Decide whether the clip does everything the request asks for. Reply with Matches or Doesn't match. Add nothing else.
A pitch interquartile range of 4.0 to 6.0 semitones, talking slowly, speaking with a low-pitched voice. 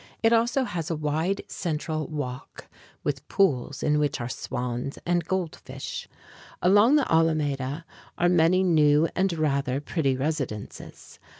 Doesn't match